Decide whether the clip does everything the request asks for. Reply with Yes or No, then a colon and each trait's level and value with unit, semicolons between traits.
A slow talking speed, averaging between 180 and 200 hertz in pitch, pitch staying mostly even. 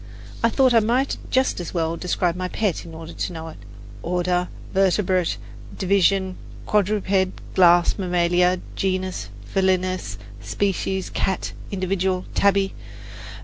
Yes: slow, 120 wpm; medium, 185 Hz; narrow, 1.8 semitones